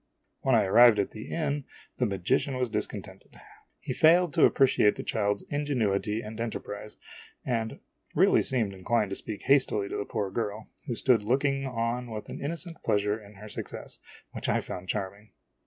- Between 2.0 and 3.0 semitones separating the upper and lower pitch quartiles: No, average, 4.2 semitones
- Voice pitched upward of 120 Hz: No, low, 110 Hz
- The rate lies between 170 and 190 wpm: Yes, average, 175 wpm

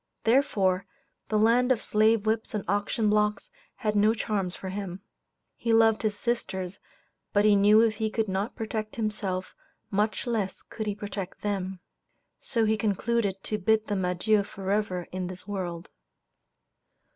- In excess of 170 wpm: No, average, 155 wpm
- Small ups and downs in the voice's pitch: Yes, narrow, 2.3 semitones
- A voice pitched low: No, high, 210 Hz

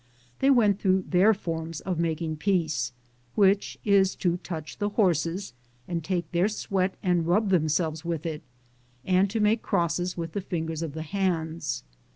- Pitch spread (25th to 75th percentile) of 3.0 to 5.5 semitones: Yes, average, 3.3 semitones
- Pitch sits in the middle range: Yes, medium, 175 Hz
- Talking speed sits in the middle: Yes, average, 165 wpm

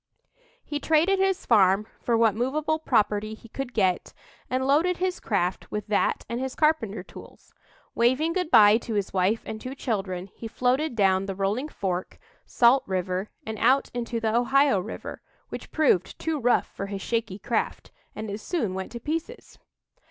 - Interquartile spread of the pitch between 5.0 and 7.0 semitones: Yes, wide, 5.6 semitones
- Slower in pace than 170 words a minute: No, average, 175 wpm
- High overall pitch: Yes, high, 230 Hz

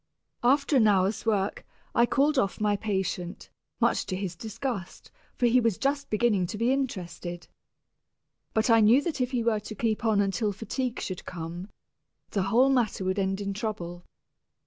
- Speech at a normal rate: Yes, average, 170 wpm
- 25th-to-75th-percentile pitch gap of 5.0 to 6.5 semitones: No, average, 3.9 semitones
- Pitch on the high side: Yes, high, 215 Hz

